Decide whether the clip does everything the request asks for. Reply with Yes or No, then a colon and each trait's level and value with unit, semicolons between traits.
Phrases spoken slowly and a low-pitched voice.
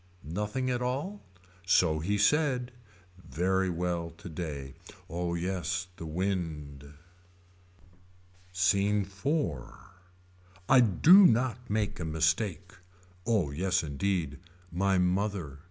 Yes: slow, 100 wpm; very low, 95 Hz